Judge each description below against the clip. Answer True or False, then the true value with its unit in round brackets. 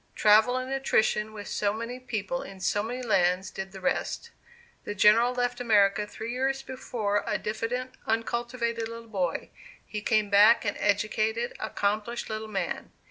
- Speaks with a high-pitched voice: True (220 Hz)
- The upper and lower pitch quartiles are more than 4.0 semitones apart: False (2.7 semitones)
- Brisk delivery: False (155 wpm)